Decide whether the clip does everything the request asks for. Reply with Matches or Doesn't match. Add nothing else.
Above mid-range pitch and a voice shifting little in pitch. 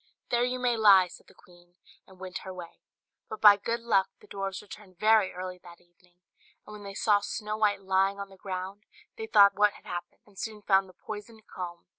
Matches